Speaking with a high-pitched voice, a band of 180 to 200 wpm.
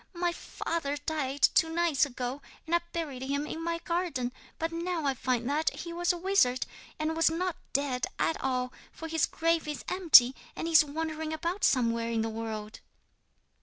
Yes: very high, 310 Hz; average, 185 wpm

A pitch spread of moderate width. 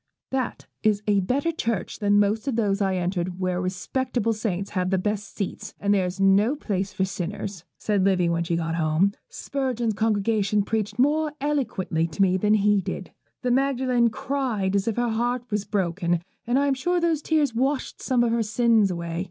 Yes: average, 4.4 semitones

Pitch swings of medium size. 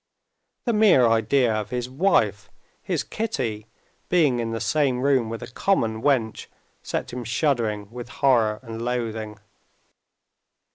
Yes: average, 3.6 semitones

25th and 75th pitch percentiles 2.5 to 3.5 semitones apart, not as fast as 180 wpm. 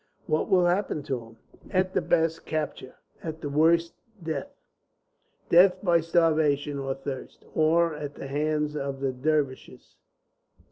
Yes: average, 3.0 semitones; average, 140 wpm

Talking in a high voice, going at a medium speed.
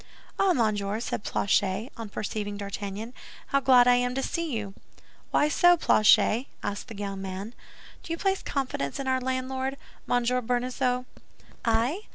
Yes: high, 245 Hz; average, 150 wpm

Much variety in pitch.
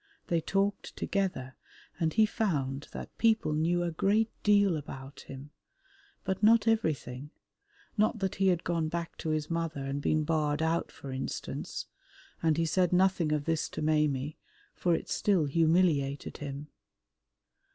No: average, 4.3 semitones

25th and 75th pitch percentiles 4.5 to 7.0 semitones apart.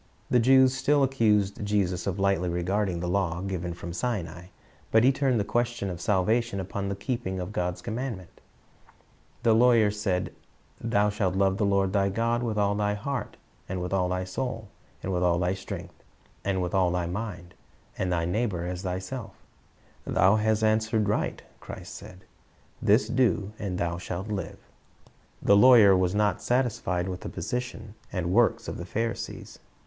No: average, 3.7 semitones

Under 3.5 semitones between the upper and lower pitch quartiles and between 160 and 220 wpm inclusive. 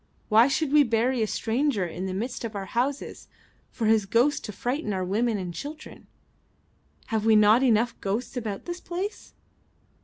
No: average, 4.2 semitones; average, 175 wpm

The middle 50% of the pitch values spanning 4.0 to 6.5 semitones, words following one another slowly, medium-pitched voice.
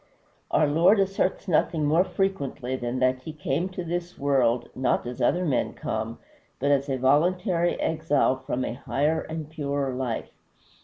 No: average, 4.7 semitones; average, 160 wpm; medium, 145 Hz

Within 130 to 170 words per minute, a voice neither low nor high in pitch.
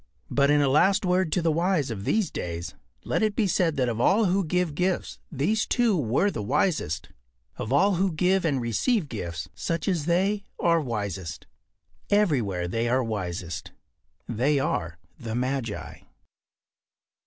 Yes: average, 160 wpm; medium, 145 Hz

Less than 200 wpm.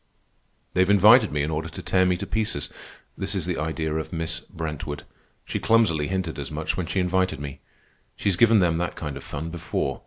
No: fast, 205 wpm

